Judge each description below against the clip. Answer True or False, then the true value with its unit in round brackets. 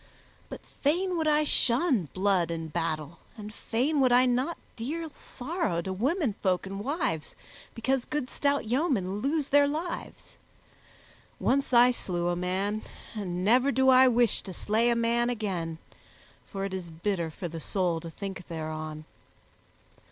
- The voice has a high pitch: True (220 Hz)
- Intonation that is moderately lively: False (6.9 semitones)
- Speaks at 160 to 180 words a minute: False (150 wpm)